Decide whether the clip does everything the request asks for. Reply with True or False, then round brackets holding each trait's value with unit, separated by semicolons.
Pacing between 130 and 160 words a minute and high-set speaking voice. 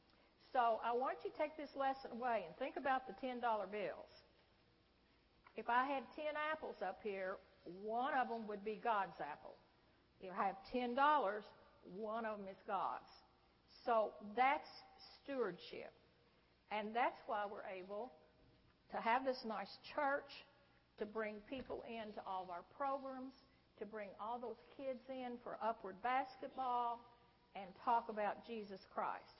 True (155 wpm; 235 Hz)